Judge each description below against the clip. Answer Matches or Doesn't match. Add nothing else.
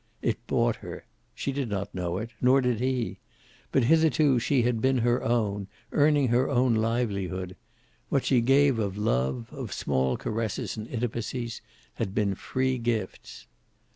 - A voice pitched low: Matches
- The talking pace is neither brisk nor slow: Matches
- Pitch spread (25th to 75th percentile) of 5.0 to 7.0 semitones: Doesn't match